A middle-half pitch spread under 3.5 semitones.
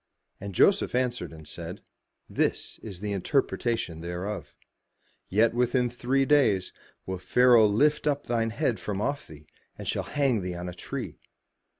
No: average, 5.2 semitones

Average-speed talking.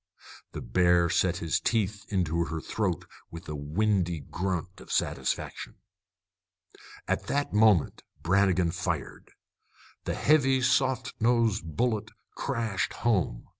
No: slow, 115 wpm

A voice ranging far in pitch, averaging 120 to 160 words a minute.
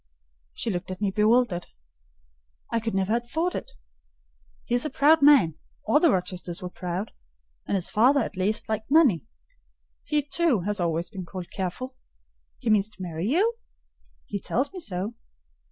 No: wide, 6.2 semitones; average, 170 wpm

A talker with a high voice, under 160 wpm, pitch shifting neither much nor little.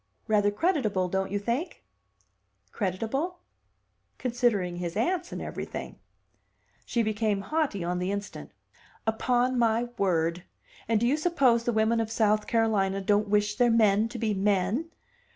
Yes: high, 220 Hz; average, 140 wpm; average, 3.3 semitones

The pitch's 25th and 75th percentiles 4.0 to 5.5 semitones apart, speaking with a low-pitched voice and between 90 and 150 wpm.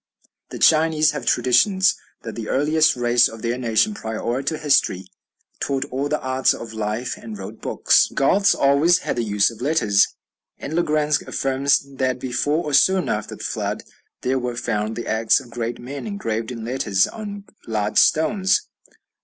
No: average, 5.1 semitones; low, 130 Hz; average, 175 wpm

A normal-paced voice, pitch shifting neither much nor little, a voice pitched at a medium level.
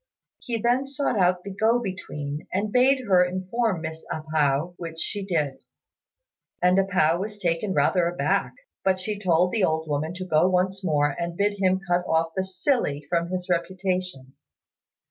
Yes: average, 175 wpm; average, 3.2 semitones; medium, 180 Hz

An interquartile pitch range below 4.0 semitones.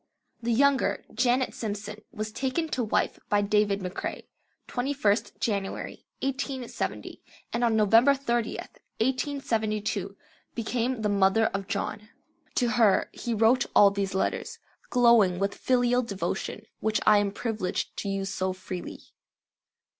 Yes: average, 3.5 semitones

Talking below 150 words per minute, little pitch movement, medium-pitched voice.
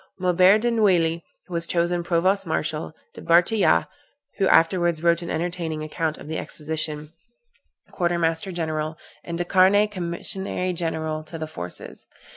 Yes: average, 140 wpm; narrow, 2.3 semitones; medium, 170 Hz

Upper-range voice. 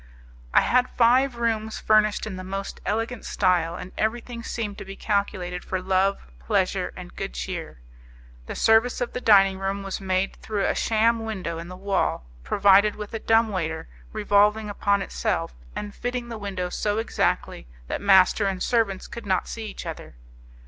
Yes: high, 205 Hz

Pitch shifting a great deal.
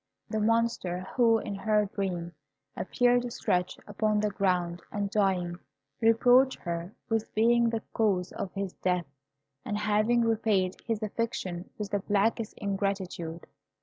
No: average, 3.5 semitones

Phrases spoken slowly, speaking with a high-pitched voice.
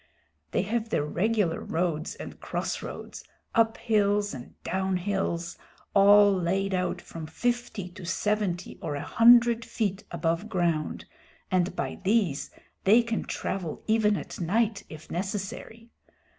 Yes: slow, 130 wpm; high, 195 Hz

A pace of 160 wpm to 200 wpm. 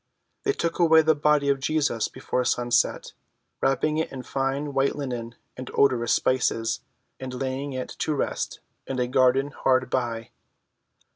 No: average, 150 wpm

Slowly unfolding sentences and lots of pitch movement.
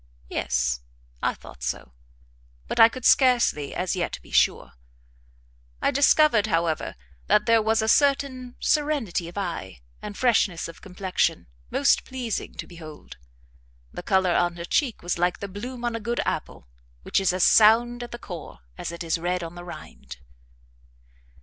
No: average, 160 wpm; wide, 5.8 semitones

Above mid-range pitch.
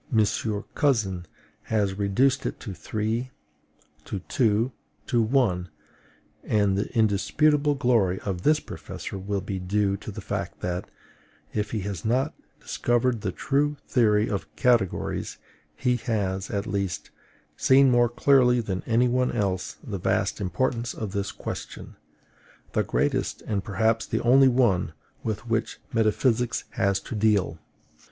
No: low, 110 Hz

